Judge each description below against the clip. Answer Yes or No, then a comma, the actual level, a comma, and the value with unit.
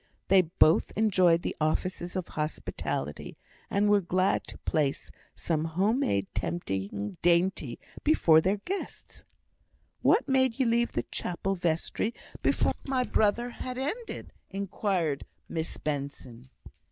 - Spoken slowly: Yes, slow, 125 wpm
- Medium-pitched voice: Yes, medium, 180 Hz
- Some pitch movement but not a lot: No, wide, 5.7 semitones